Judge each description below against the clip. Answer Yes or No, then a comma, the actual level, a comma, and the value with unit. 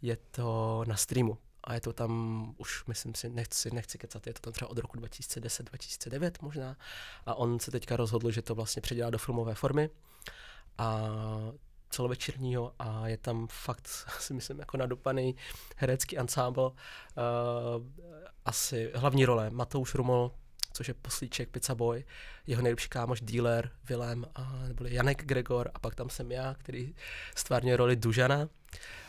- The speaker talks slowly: No, average, 155 wpm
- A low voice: Yes, low, 120 Hz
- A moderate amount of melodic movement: No, narrow, 1.9 semitones